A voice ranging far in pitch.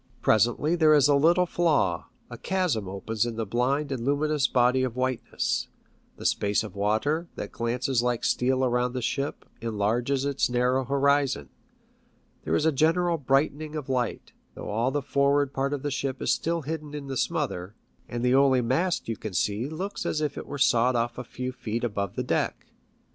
No: average, 3.7 semitones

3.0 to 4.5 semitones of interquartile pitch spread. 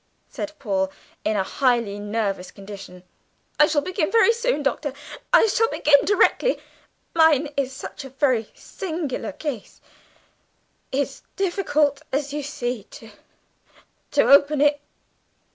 No: average, 5.3 semitones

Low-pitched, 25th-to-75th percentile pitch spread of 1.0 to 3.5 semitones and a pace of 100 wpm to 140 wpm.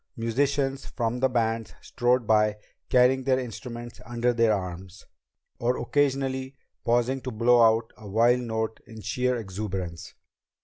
Yes: low, 120 Hz; narrow, 2.4 semitones; slow, 135 wpm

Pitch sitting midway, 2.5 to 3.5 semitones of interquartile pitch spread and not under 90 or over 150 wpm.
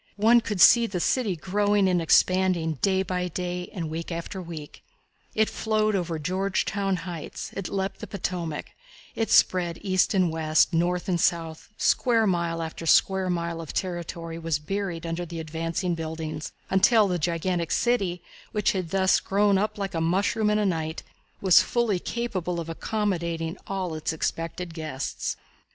No: medium, 180 Hz; average, 3.0 semitones; average, 160 wpm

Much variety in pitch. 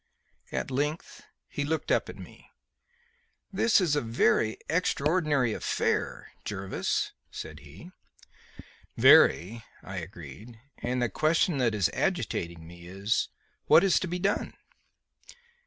Yes: wide, 8.4 semitones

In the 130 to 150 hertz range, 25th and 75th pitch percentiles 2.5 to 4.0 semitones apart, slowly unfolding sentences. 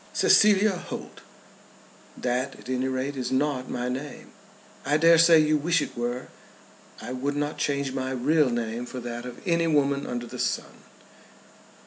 No: low, 135 Hz; average, 3.3 semitones; average, 165 wpm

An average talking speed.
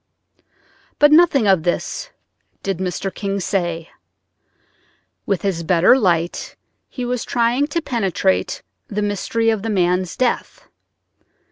No: slow, 120 wpm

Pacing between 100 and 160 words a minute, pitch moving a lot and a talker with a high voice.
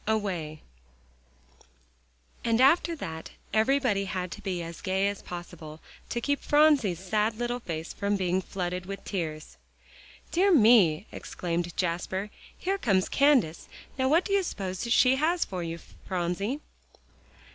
Yes: average, 140 wpm; wide, 6.2 semitones; high, 195 Hz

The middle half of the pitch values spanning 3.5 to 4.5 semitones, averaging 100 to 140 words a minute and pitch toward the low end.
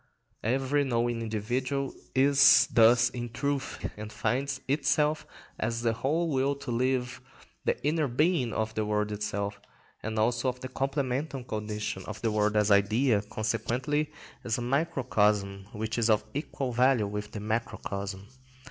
No: average, 4.0 semitones; average, 150 wpm; low, 120 Hz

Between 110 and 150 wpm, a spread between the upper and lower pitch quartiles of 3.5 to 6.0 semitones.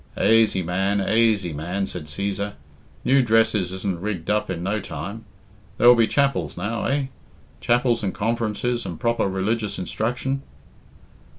Yes: slow, 135 wpm; average, 3.8 semitones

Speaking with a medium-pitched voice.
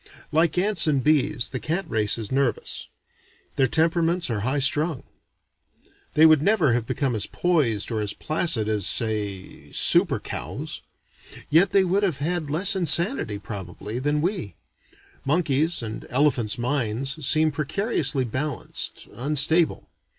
Yes: medium, 145 Hz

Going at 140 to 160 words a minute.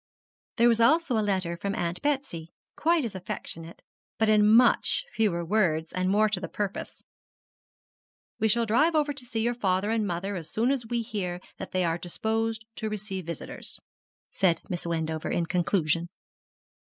No: average, 170 wpm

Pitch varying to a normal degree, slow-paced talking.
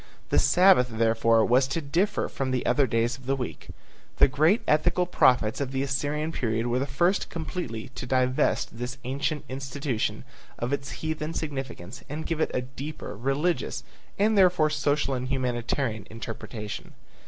No: average, 3.8 semitones; average, 160 wpm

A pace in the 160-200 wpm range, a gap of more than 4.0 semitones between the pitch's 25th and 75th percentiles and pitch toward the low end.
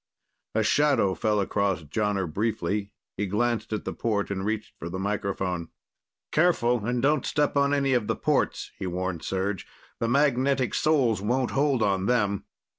Yes: average, 165 wpm; average, 4.7 semitones; low, 110 Hz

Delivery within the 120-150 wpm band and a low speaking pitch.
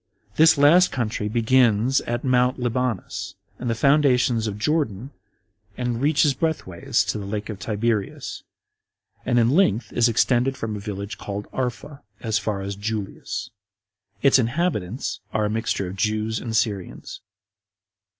Yes: average, 140 wpm; low, 115 Hz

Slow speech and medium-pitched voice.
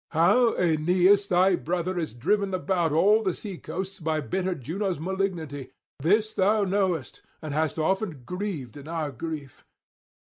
No: average, 145 wpm; medium, 180 Hz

